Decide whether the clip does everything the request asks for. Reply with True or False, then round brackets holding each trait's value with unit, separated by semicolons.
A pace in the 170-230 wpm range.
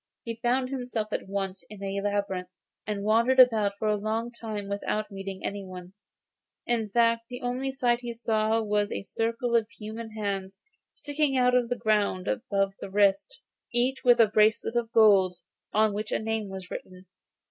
True (175 wpm)